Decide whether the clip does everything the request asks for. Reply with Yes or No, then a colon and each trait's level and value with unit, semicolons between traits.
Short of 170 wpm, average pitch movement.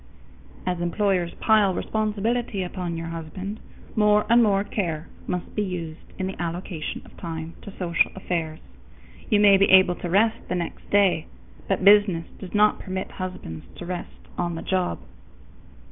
Yes: average, 160 wpm; average, 3.1 semitones